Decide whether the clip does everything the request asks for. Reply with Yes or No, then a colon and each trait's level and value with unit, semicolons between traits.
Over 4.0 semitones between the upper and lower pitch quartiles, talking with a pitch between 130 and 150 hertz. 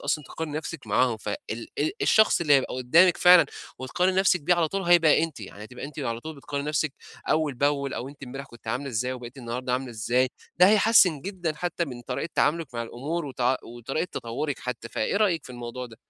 Yes: average, 5.0 semitones; medium, 140 Hz